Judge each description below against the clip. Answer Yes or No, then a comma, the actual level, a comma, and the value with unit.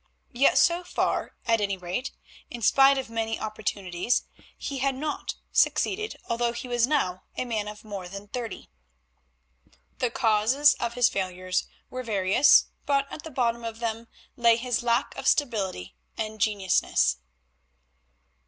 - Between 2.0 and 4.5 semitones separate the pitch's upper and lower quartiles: Yes, average, 3.7 semitones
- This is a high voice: Yes, high, 230 Hz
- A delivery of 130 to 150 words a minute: Yes, average, 145 wpm